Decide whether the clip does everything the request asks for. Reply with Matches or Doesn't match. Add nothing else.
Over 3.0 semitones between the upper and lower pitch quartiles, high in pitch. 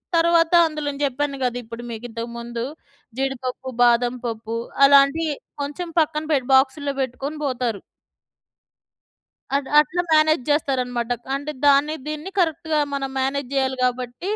Matches